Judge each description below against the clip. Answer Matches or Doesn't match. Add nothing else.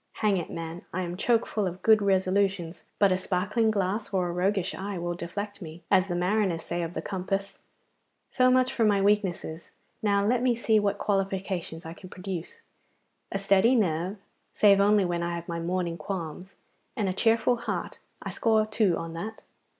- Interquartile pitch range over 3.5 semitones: Doesn't match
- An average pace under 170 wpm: Doesn't match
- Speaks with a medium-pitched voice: Doesn't match